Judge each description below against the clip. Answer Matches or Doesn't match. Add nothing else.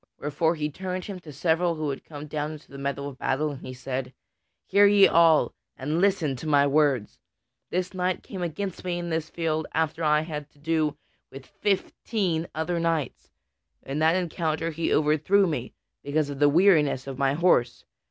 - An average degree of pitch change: Matches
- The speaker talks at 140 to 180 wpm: Doesn't match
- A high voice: Doesn't match